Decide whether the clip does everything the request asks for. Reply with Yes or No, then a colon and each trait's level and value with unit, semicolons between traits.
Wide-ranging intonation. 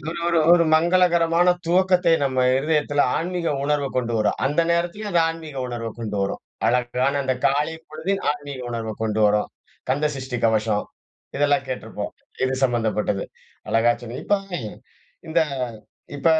Yes: wide, 5.7 semitones